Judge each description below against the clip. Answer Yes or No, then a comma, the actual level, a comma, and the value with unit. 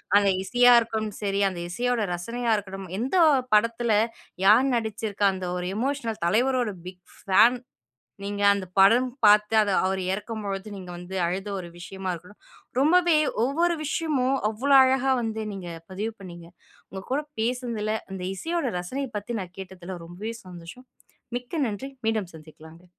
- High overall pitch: Yes, high, 210 Hz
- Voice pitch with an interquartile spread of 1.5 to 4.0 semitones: No, average, 4.5 semitones